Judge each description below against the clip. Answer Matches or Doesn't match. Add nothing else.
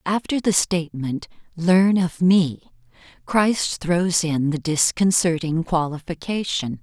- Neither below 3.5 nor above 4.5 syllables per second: Matches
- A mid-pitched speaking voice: Matches